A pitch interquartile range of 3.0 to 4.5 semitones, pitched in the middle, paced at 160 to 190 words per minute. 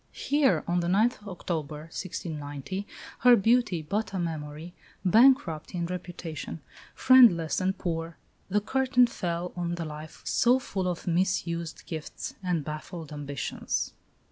No: average, 4.0 semitones; medium, 175 Hz; slow, 135 wpm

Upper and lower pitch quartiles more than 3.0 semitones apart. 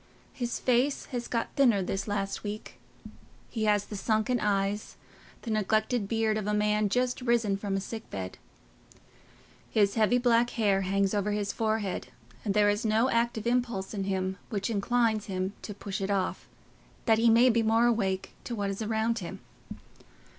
No: average, 2.7 semitones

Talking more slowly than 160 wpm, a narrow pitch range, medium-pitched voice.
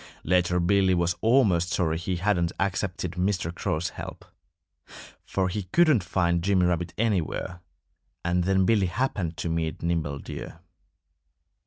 No: slow, 135 wpm; narrow, 2.2 semitones; very low, 90 Hz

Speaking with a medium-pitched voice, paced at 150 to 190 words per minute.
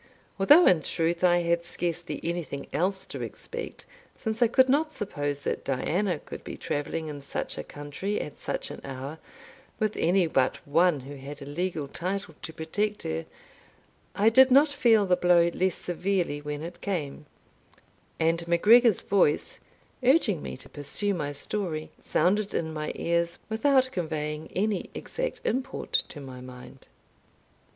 Yes: medium, 170 Hz; average, 155 wpm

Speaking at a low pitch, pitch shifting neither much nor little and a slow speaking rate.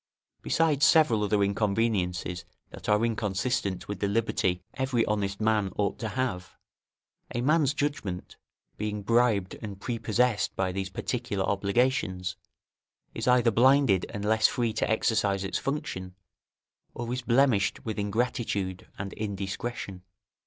Yes: low, 105 Hz; average, 3.7 semitones; slow, 130 wpm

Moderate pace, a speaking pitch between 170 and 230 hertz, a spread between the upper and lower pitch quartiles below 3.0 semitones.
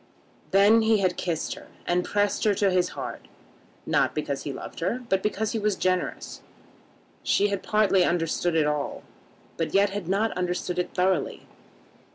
Yes: average, 170 wpm; high, 190 Hz; narrow, 2.5 semitones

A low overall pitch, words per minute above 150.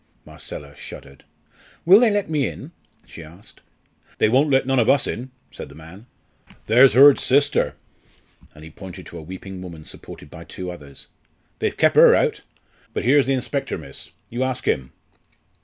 Yes: low, 115 Hz; average, 175 wpm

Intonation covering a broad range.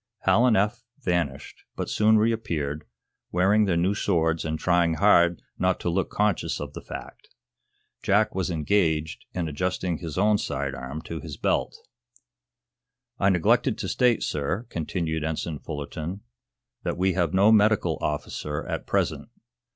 No: average, 4.4 semitones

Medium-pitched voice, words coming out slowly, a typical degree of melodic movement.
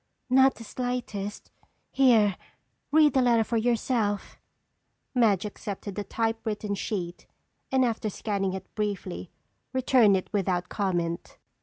No: high, 210 Hz; slow, 120 wpm; average, 3.8 semitones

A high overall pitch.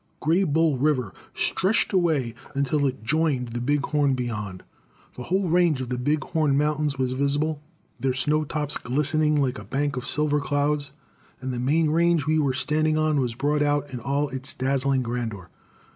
No: medium, 145 Hz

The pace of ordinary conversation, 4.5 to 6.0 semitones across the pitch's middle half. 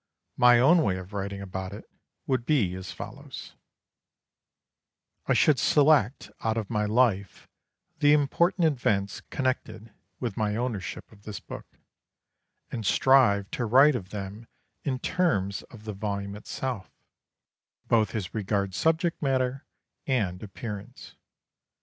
No: slow, 130 wpm; average, 4.8 semitones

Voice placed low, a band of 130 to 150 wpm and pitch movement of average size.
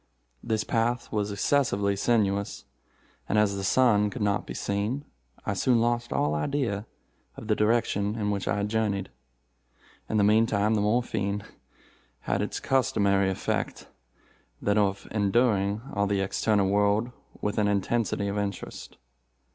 No: low, 105 Hz; average, 140 wpm; narrow, 2.1 semitones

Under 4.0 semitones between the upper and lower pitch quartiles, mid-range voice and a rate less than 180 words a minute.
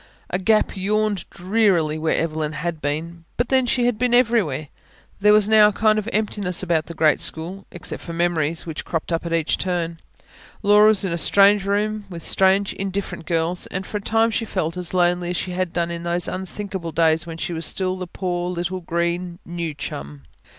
No: average, 3.4 semitones; medium, 180 Hz; fast, 205 wpm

